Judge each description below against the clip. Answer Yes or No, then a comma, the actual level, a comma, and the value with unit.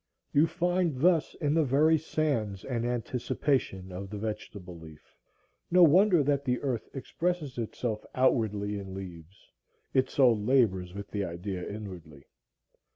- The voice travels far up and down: Yes, wide, 6.8 semitones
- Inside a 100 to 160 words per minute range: Yes, average, 140 wpm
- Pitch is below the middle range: Yes, low, 115 Hz